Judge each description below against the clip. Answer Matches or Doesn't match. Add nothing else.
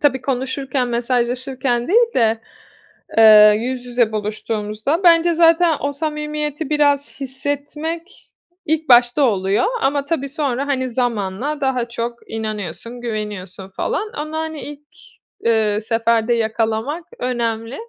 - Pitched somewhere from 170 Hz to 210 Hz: Doesn't match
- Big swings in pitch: Doesn't match